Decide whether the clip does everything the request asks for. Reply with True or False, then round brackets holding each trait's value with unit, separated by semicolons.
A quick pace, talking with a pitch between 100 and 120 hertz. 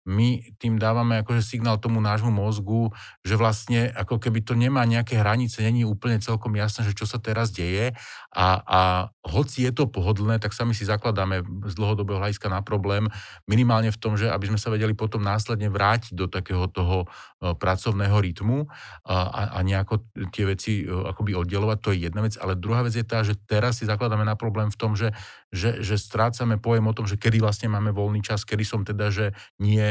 True (200 wpm; 110 Hz)